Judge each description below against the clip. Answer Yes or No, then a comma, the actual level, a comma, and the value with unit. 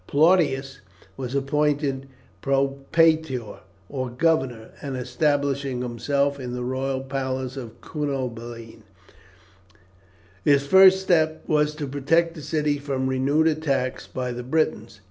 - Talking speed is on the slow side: Yes, slow, 115 wpm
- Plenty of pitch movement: No, narrow, 2.6 semitones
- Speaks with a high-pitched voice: No, low, 135 Hz